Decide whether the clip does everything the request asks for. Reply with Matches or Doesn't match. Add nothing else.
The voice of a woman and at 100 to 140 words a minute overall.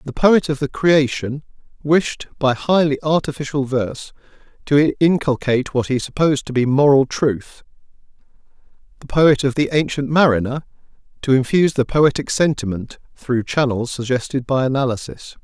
Doesn't match